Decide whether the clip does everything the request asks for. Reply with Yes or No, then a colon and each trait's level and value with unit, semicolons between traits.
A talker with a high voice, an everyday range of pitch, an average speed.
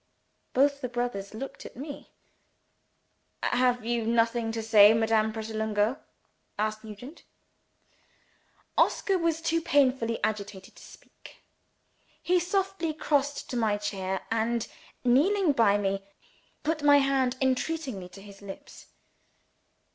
No: high, 235 Hz; average, 4.9 semitones; slow, 115 wpm